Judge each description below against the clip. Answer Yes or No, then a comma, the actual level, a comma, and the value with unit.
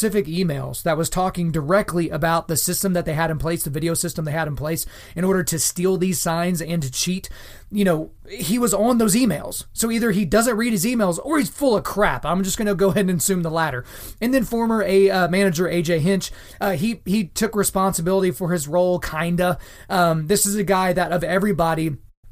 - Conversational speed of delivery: No, fast, 225 wpm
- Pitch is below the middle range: No, medium, 180 Hz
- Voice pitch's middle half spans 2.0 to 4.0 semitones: Yes, average, 3.2 semitones